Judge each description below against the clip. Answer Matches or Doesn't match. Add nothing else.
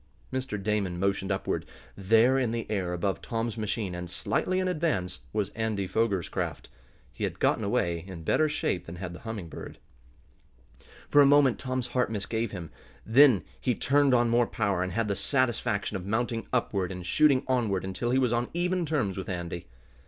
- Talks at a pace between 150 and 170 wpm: Doesn't match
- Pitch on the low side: Matches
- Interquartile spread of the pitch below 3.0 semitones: Doesn't match